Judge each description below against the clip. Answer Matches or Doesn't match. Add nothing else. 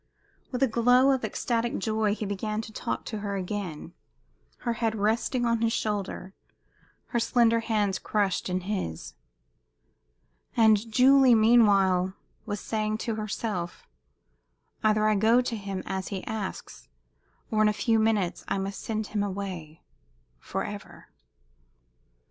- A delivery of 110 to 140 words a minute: Matches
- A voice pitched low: Doesn't match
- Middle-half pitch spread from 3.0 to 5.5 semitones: Doesn't match